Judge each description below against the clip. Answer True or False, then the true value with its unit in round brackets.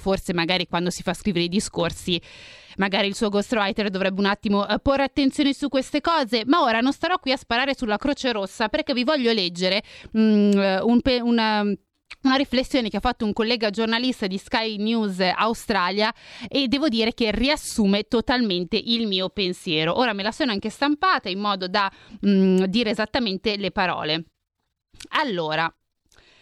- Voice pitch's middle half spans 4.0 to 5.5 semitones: True (4.6 semitones)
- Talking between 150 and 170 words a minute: True (165 wpm)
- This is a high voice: True (220 Hz)